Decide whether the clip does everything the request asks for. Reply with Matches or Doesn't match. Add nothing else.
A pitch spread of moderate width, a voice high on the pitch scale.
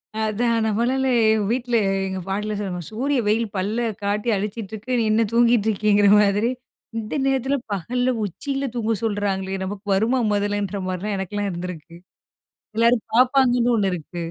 Matches